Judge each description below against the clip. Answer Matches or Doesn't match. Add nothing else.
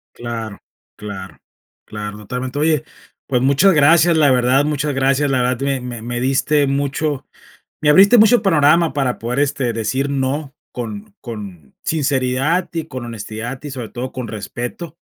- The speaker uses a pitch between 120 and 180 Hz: Matches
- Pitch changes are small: Doesn't match